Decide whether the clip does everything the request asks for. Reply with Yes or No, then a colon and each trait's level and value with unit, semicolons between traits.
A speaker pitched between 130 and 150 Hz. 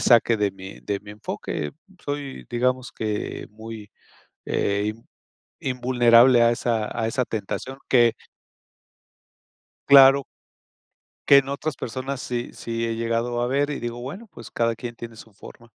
No: low, 120 Hz